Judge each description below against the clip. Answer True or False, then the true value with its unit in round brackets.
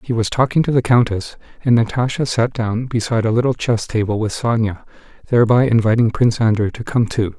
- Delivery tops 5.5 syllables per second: True (5.9 syllables/s)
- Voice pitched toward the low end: True (115 Hz)